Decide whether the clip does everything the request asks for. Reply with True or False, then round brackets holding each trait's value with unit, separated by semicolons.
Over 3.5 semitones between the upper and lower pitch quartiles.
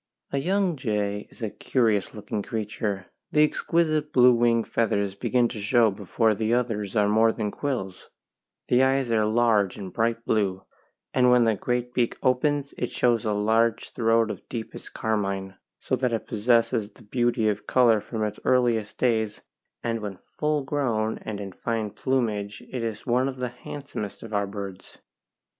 False (3.0 semitones)